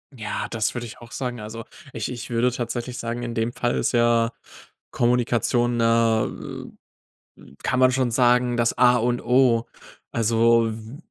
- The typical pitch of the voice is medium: No, low, 120 Hz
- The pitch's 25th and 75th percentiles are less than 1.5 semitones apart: Yes, narrow, 1.1 semitones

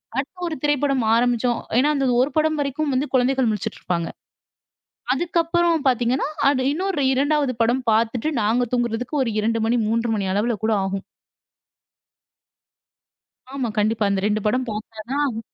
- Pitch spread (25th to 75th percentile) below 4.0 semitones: No, average, 4.3 semitones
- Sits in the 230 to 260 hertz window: Yes, very high, 250 Hz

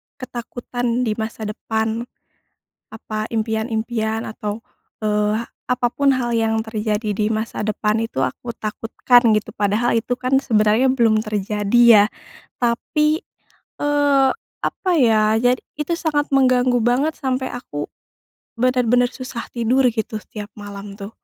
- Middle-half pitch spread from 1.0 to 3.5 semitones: Yes, average, 2.7 semitones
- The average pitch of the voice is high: Yes, high, 230 Hz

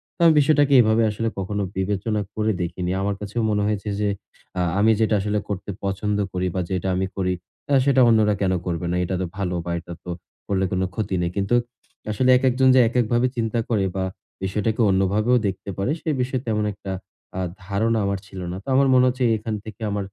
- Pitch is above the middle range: No, low, 105 Hz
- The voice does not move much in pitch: No, average, 3.2 semitones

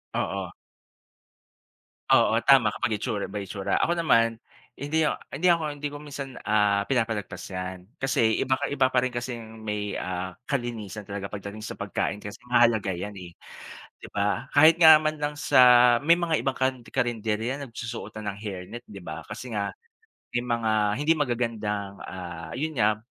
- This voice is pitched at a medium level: No, low, 115 Hz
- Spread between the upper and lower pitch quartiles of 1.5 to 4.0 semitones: No, average, 4.7 semitones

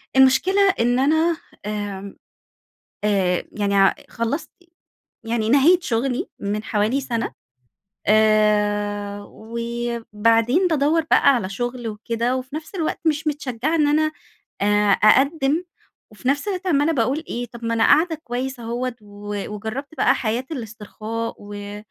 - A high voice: Yes, high, 235 Hz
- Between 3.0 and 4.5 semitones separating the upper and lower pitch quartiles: No, average, 5.1 semitones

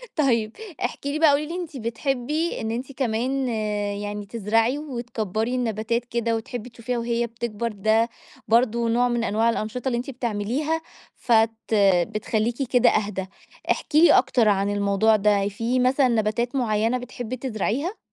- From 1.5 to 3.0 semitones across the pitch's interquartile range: Yes, narrow, 2.6 semitones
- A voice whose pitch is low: No, high, 235 Hz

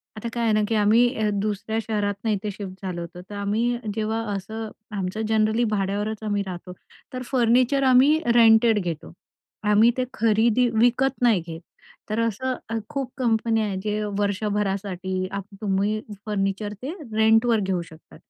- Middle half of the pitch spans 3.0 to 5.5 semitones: No, narrow, 2.4 semitones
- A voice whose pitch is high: Yes, high, 215 Hz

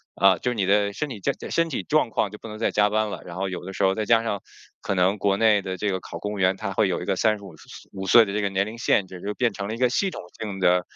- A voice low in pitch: Yes, low, 100 Hz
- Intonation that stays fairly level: Yes, narrow, 2.3 semitones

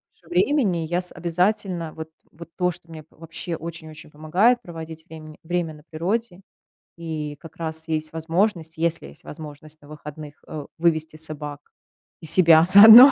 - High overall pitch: No, medium, 165 Hz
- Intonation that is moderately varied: No, narrow, 2.2 semitones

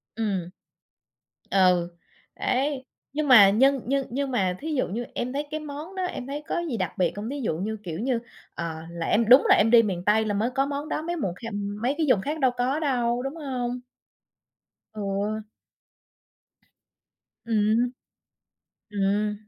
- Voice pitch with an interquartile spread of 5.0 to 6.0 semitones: Yes, average, 5.3 semitones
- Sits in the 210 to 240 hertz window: Yes, high, 235 Hz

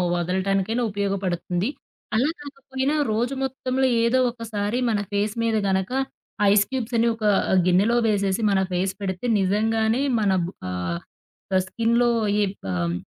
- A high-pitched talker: Yes, high, 210 Hz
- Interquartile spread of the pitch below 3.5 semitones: No, average, 3.8 semitones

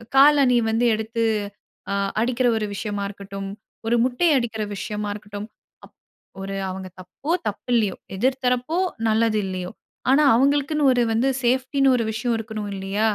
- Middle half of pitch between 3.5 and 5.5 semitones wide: Yes, average, 3.8 semitones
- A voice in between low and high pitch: No, high, 225 Hz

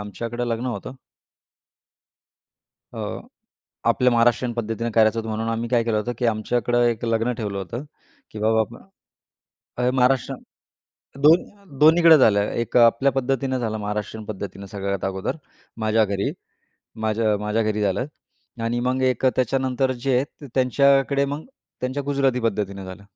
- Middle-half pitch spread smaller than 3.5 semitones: Yes, average, 3.1 semitones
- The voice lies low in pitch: Yes, low, 115 Hz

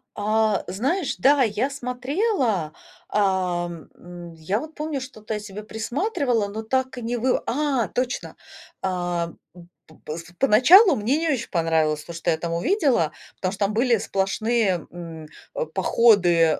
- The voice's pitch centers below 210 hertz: No, high, 215 Hz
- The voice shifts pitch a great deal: Yes, wide, 6.8 semitones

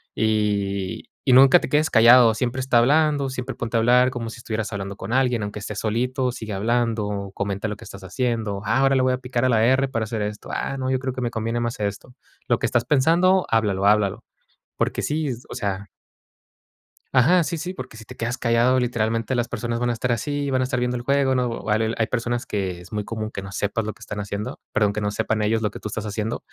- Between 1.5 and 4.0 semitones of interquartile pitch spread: Yes, average, 3.4 semitones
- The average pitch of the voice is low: Yes, low, 115 Hz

